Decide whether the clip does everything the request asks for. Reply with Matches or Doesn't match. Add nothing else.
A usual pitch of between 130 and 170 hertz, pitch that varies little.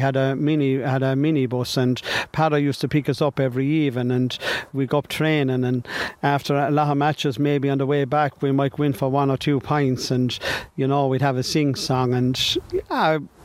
Matches